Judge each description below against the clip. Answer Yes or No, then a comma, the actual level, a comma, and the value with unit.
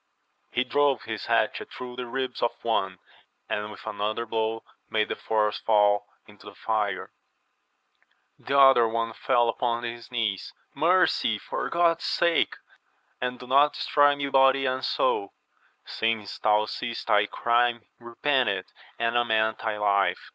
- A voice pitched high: No, low, 115 Hz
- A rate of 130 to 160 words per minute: Yes, average, 145 wpm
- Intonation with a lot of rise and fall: No, average, 3.6 semitones